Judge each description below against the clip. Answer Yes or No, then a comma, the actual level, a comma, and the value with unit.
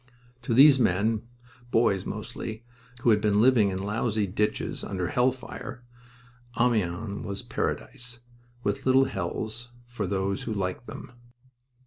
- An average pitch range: Yes, average, 3.4 semitones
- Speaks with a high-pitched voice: No, low, 110 Hz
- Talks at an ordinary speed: No, slow, 130 wpm